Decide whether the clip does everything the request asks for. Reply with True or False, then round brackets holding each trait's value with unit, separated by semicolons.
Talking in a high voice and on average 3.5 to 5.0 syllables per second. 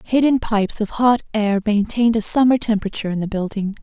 False (215 Hz; 6.3 syllables/s)